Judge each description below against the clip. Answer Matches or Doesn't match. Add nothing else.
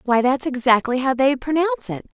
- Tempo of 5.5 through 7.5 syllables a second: Matches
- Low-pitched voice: Doesn't match